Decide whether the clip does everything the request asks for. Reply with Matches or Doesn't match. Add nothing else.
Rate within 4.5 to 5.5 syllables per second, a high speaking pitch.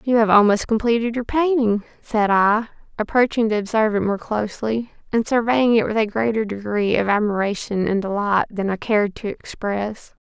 Matches